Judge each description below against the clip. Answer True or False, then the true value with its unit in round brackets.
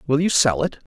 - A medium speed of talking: False (255 wpm)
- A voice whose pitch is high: False (140 Hz)